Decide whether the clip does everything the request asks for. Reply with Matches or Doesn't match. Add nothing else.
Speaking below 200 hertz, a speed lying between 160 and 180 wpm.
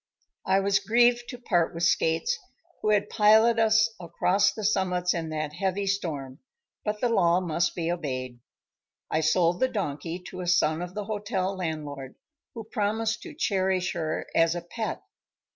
Matches